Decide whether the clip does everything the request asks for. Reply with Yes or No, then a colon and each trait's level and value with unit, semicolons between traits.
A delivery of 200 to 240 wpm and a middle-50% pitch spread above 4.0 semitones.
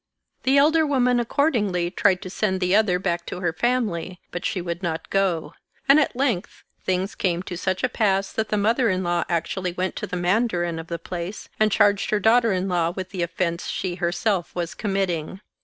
No: fast, 205 wpm; average, 3.7 semitones